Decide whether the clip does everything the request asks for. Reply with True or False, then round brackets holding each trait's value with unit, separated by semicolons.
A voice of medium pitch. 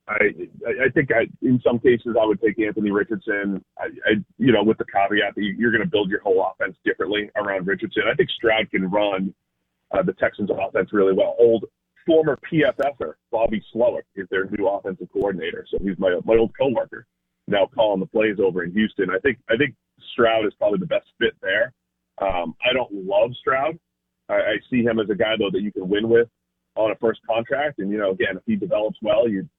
False (105 Hz)